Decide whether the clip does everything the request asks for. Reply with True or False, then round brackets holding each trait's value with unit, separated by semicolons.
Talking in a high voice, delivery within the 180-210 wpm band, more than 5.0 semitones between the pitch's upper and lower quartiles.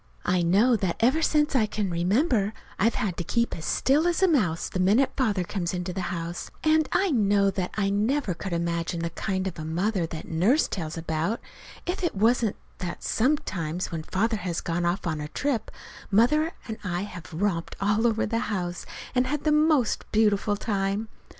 True (200 Hz; 195 wpm; 5.4 semitones)